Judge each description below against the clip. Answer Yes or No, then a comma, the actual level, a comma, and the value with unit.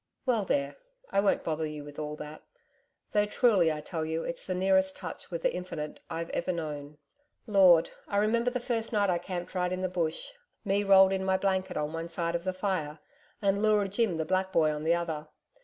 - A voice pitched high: No, medium, 180 Hz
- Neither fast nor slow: No, fast, 215 wpm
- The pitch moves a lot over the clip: No, average, 3.6 semitones